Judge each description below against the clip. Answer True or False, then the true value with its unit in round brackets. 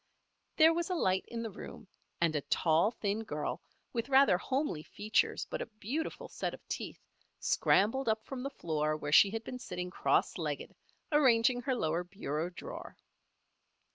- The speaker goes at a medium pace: True (170 wpm)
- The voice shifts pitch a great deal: True (7.1 semitones)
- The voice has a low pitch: False (215 Hz)